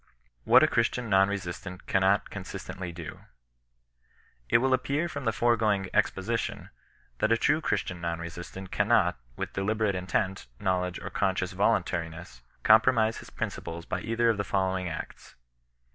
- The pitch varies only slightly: No, average, 3.8 semitones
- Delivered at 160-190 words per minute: No, average, 150 wpm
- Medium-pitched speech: No, very low, 95 Hz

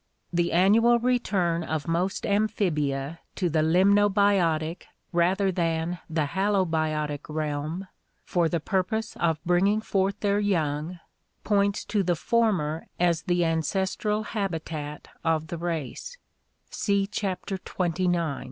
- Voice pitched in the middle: Yes, medium, 175 Hz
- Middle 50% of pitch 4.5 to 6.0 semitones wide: No, average, 3.8 semitones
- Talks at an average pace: No, slow, 115 wpm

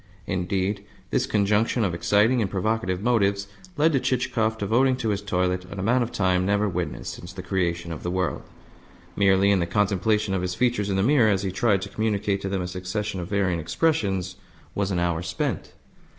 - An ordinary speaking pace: Yes, average, 195 wpm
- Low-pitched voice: Yes, low, 100 Hz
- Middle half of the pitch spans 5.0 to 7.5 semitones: No, average, 2.8 semitones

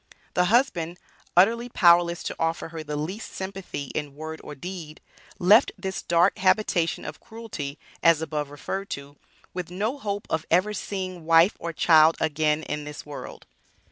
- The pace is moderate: Yes, average, 160 wpm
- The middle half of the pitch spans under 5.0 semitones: Yes, average, 3.7 semitones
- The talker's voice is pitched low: No, medium, 170 Hz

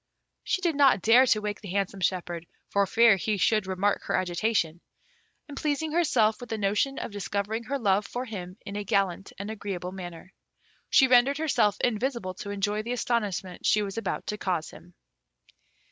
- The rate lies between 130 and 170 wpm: No, average, 180 wpm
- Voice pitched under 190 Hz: No, high, 205 Hz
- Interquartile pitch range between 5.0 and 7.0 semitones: No, average, 3.8 semitones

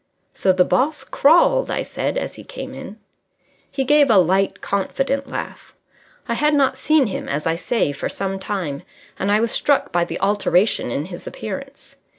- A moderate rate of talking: Yes, average, 180 wpm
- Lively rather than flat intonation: Yes, wide, 6.8 semitones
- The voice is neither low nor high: No, high, 210 Hz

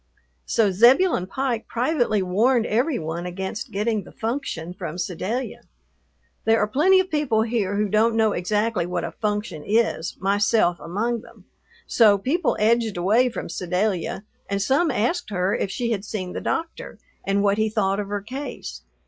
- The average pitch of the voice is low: No, high, 215 Hz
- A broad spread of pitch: No, average, 3.7 semitones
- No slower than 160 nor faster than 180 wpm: Yes, average, 165 wpm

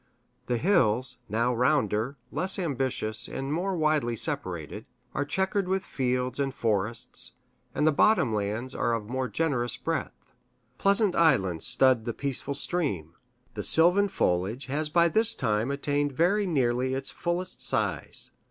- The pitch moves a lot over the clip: Yes, wide, 6.1 semitones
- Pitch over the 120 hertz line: Yes, low, 135 Hz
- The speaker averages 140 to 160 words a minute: Yes, average, 145 wpm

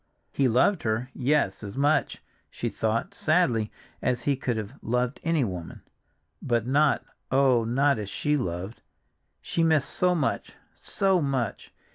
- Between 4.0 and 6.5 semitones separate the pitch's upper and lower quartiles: Yes, average, 4.7 semitones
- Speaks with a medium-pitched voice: No, low, 130 Hz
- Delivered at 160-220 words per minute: No, average, 140 wpm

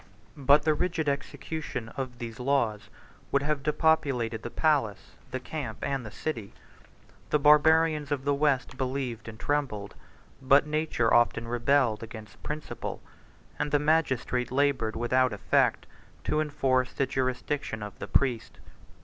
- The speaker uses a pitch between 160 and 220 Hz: No, low, 135 Hz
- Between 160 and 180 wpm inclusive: No, average, 140 wpm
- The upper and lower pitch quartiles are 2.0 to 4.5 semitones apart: Yes, average, 3.8 semitones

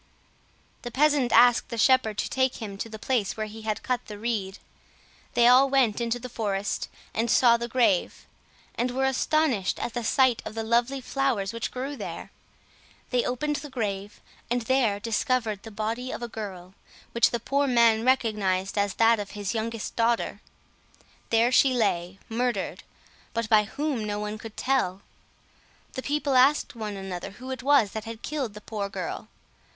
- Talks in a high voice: Yes, high, 230 Hz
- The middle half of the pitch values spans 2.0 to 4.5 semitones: Yes, average, 3.4 semitones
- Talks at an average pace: Yes, average, 175 wpm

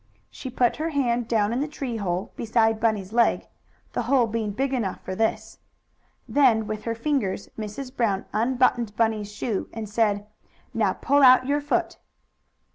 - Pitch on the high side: Yes, high, 230 Hz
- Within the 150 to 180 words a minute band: Yes, average, 165 wpm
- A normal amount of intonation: Yes, average, 3.2 semitones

